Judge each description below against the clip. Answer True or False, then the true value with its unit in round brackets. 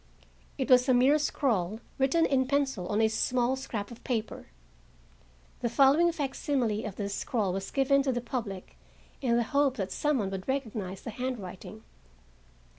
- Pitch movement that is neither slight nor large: True (4.3 semitones)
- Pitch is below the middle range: False (245 Hz)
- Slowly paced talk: False (165 wpm)